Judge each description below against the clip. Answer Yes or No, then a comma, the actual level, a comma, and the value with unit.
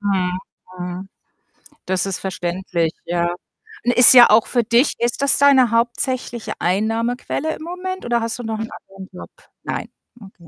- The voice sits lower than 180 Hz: No, high, 225 Hz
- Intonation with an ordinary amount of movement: Yes, average, 4.6 semitones